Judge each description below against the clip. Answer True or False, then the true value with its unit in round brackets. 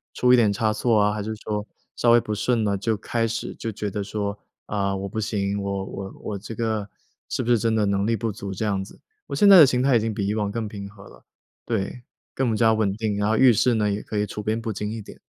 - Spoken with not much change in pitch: True (2.1 semitones)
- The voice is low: True (105 Hz)